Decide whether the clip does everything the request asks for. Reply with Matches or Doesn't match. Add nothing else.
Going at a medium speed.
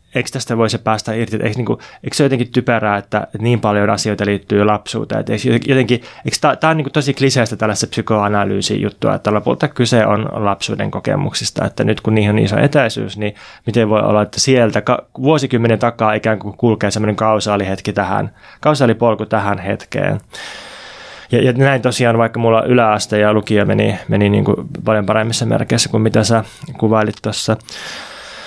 Doesn't match